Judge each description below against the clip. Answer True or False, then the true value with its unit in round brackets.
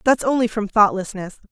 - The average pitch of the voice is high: True (215 Hz)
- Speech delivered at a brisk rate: False (160 wpm)